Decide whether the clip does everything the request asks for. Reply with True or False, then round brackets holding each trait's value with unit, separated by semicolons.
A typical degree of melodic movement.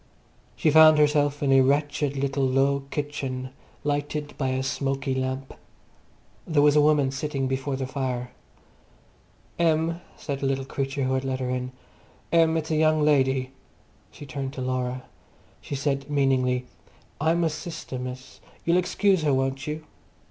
False (2.2 semitones)